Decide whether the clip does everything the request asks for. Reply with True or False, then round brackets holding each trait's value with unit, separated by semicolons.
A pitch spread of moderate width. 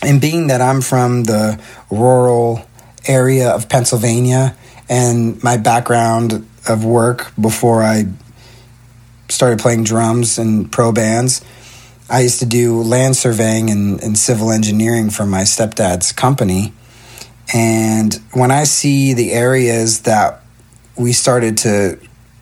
False (1.8 semitones)